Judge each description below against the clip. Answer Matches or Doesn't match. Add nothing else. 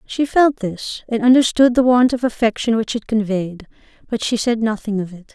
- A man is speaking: Doesn't match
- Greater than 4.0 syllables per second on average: Matches